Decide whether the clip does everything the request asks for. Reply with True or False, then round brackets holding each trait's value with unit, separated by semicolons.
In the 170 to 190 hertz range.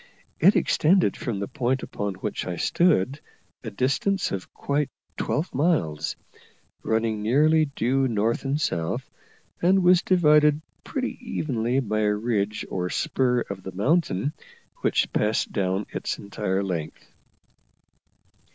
False (120 Hz)